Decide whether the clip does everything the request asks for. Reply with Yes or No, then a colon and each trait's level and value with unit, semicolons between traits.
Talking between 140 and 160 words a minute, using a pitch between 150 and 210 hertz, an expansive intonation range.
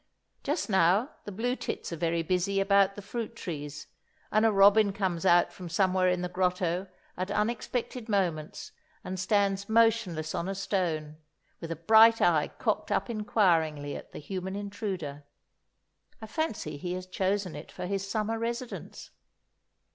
No: average, 155 wpm; high, 190 Hz; average, 3.6 semitones